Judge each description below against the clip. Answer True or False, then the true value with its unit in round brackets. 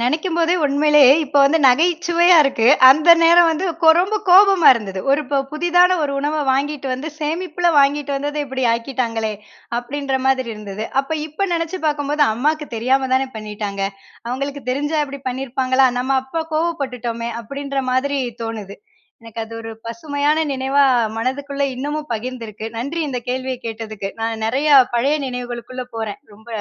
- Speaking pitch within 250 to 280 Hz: True (275 Hz)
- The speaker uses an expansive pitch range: False (4.1 semitones)